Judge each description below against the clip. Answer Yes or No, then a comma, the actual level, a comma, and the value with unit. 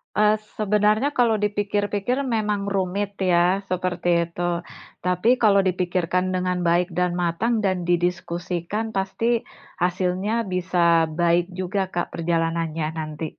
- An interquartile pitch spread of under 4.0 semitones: Yes, average, 2.9 semitones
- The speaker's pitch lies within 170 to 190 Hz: Yes, medium, 185 Hz